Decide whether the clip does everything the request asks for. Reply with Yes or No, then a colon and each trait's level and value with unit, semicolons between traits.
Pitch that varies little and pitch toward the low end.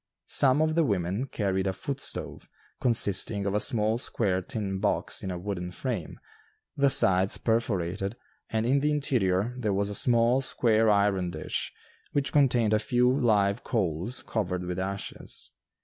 No: average, 4.4 semitones; low, 105 Hz